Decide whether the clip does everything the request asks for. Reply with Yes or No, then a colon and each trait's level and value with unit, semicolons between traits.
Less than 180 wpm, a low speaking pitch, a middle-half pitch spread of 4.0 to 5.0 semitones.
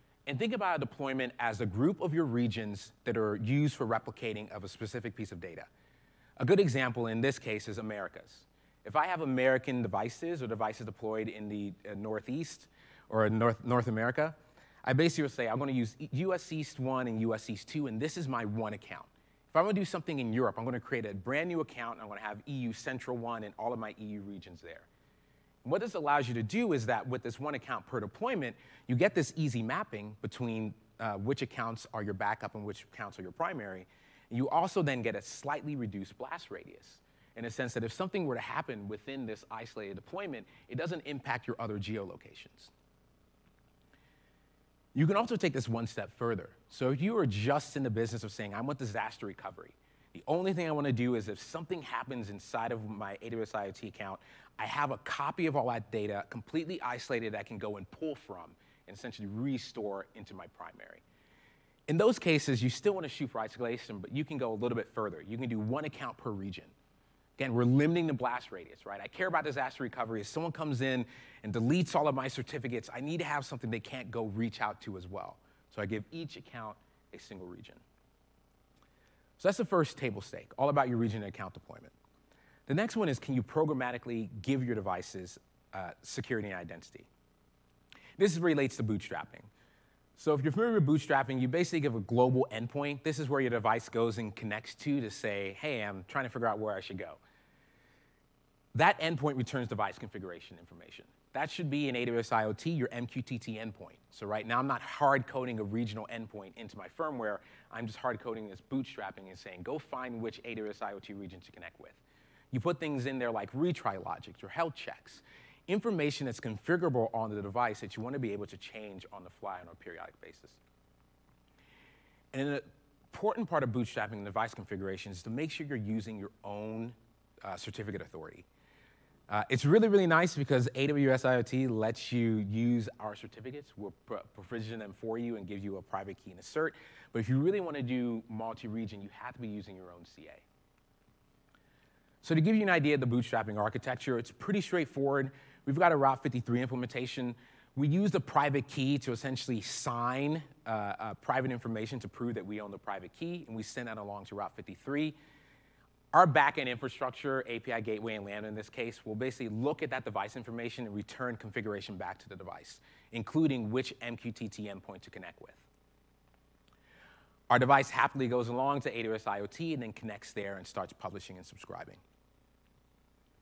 No: average, 200 wpm; low, 120 Hz; average, 4.5 semitones